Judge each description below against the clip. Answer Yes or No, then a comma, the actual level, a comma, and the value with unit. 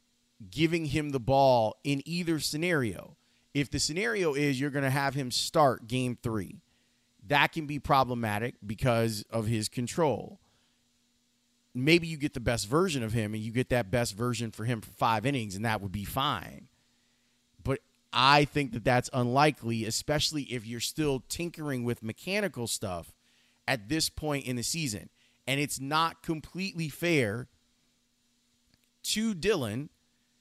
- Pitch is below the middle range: Yes, low, 125 Hz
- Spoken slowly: No, average, 155 wpm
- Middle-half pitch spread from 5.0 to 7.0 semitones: No, average, 3.5 semitones